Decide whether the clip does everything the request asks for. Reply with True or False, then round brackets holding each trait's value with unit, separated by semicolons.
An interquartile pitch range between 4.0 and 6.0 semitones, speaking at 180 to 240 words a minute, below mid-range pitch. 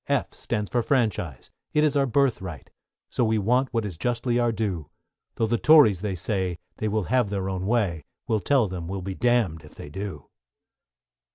True (4.5 semitones; 190 wpm; 105 Hz)